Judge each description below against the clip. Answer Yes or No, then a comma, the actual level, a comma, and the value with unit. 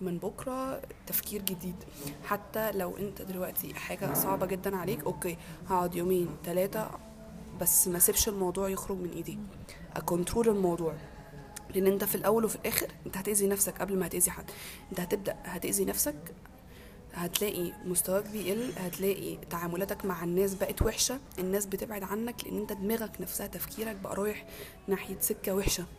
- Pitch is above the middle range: Yes, high, 195 Hz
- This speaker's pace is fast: Yes, fast, 150 wpm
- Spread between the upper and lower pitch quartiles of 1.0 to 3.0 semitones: Yes, narrow, 2.4 semitones